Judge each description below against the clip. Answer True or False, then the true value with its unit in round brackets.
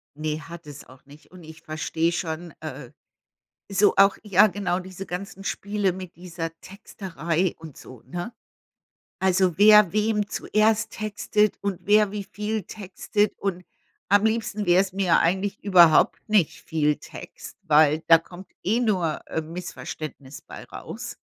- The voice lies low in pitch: False (185 Hz)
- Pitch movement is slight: False (3.9 semitones)